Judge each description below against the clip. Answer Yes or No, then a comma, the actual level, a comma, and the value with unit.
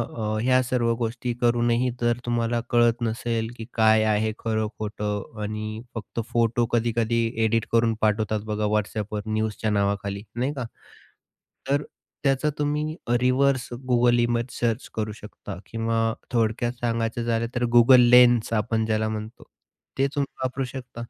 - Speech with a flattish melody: Yes, narrow, 1.8 semitones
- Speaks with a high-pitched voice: No, low, 115 Hz